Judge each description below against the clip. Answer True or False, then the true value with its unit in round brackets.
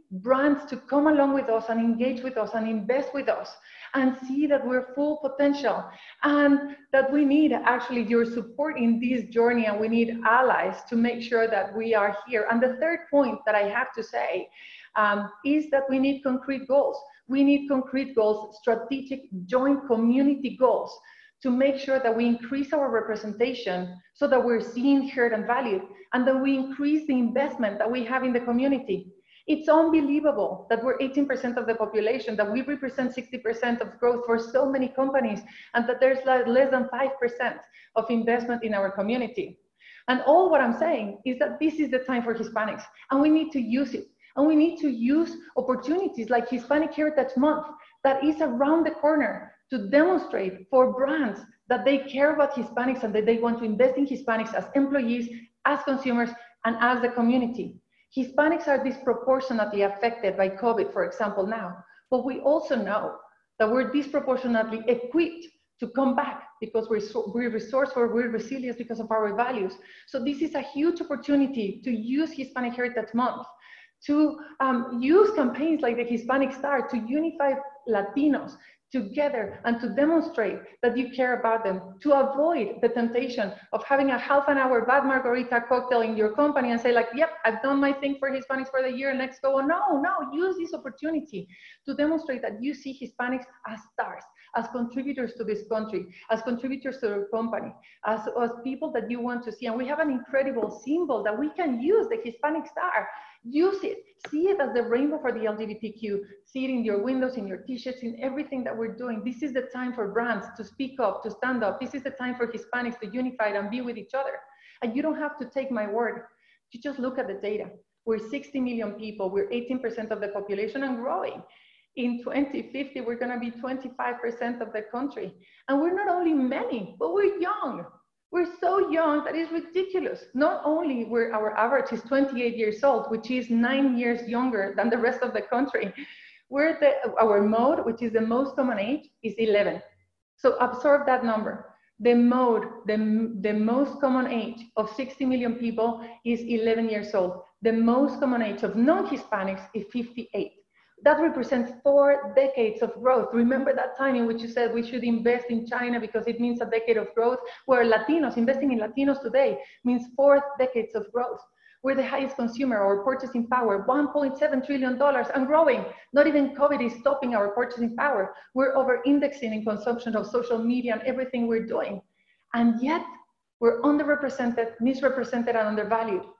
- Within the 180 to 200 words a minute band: True (185 wpm)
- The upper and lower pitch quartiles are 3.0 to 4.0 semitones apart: True (3.4 semitones)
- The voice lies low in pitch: False (250 Hz)